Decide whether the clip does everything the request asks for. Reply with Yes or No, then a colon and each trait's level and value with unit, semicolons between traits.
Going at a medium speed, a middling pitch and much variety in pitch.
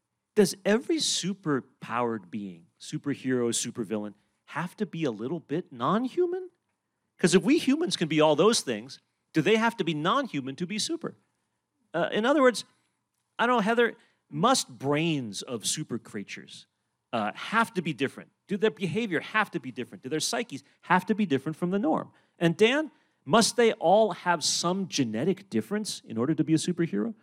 Yes: average, 185 wpm; medium, 180 Hz; wide, 7.8 semitones